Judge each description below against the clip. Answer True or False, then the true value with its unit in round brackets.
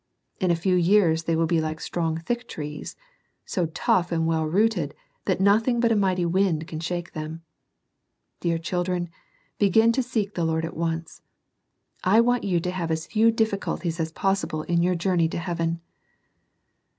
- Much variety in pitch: False (3.3 semitones)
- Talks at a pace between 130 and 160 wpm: False (175 wpm)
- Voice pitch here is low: False (175 Hz)